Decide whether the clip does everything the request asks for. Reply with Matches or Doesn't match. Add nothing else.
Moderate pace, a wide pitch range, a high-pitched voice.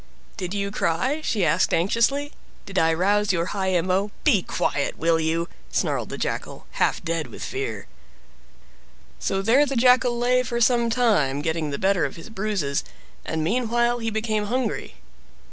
Matches